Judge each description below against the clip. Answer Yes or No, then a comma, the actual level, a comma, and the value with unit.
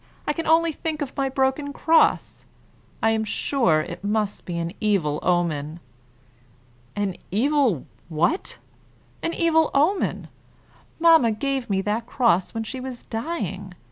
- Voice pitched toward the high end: Yes, high, 230 Hz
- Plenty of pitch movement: Yes, wide, 7.2 semitones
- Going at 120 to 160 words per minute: Yes, average, 140 wpm